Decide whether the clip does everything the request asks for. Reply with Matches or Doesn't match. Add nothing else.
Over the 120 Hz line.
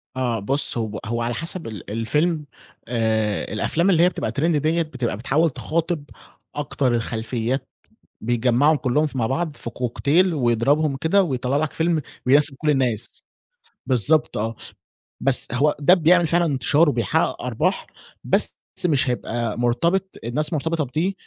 Matches